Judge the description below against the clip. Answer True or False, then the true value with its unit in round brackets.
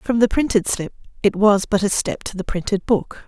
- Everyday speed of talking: False (240 wpm)